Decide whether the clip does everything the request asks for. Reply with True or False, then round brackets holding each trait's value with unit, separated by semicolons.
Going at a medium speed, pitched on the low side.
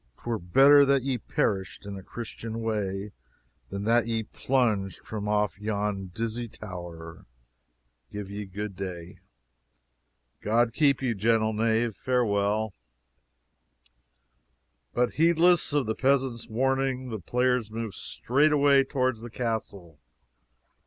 False (120 wpm; 115 Hz)